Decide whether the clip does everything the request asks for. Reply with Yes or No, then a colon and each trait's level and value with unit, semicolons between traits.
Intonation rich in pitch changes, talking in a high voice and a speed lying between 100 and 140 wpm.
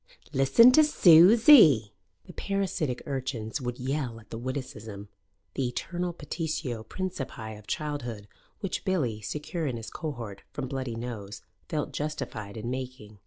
No: wide, 5.9 semitones; low, 130 Hz; slow, 135 wpm